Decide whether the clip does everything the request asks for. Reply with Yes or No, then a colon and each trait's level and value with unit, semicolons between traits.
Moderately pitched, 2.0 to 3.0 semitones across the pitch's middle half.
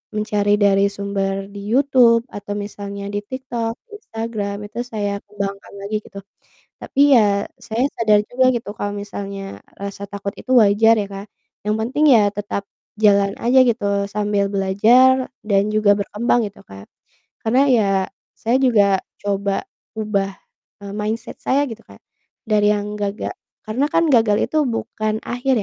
No: high, 210 Hz; narrow, 2.4 semitones